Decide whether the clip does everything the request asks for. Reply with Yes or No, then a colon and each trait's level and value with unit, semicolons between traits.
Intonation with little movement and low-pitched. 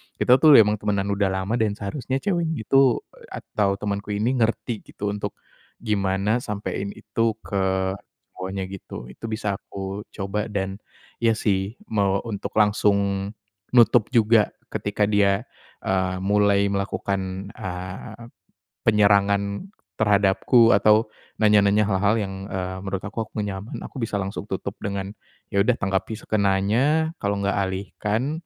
Yes: narrow, 1.9 semitones; low, 100 Hz